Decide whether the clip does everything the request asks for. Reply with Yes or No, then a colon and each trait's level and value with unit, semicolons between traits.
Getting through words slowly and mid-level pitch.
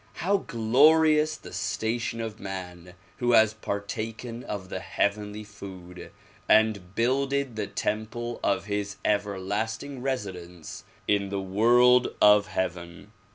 No: slow, 120 wpm; low, 105 Hz